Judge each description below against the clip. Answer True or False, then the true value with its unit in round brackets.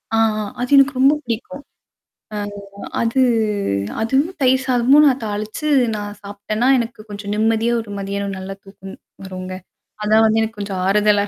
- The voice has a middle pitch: False (220 Hz)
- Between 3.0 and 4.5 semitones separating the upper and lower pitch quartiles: True (3.8 semitones)